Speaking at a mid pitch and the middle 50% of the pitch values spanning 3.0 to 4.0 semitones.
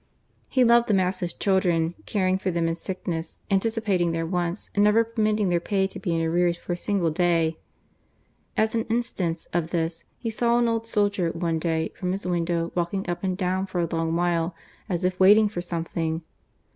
Yes: medium, 180 Hz; average, 3.3 semitones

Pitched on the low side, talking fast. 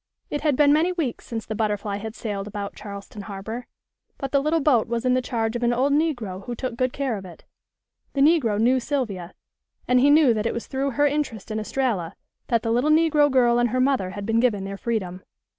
No: high, 240 Hz; fast, 225 wpm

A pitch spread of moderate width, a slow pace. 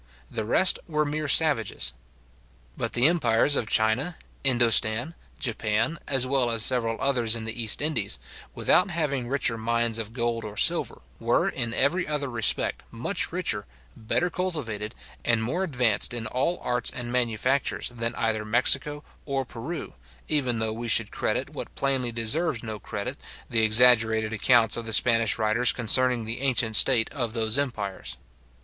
No: average, 3.5 semitones; average, 155 wpm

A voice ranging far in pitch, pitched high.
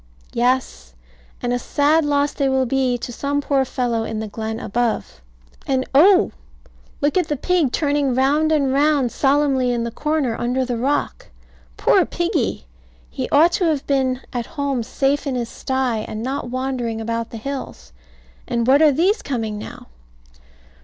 No: average, 3.3 semitones; very high, 265 Hz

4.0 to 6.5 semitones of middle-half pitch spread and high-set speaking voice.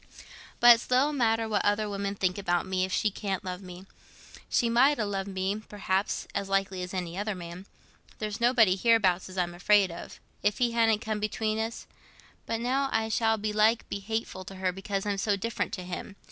No: average, 2.9 semitones; high, 205 Hz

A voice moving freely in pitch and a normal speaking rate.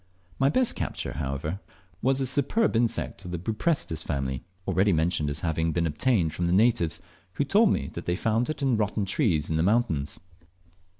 Yes: wide, 7.4 semitones; average, 180 wpm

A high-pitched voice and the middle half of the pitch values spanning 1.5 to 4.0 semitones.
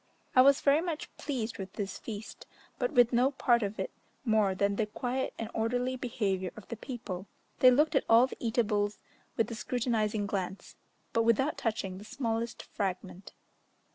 Yes: high, 225 Hz; average, 3.4 semitones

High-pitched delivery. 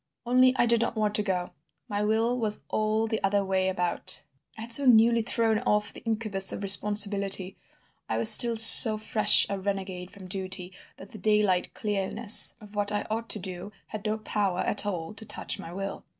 Yes: high, 210 Hz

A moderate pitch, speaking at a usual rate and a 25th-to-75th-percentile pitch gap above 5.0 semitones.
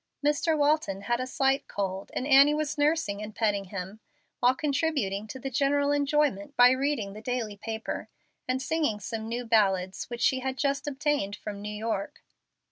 No: high, 245 Hz; average, 175 wpm; wide, 5.5 semitones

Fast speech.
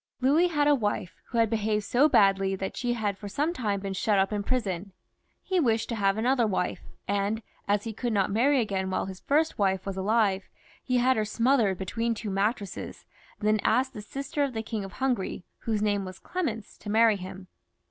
Yes: fast, 210 wpm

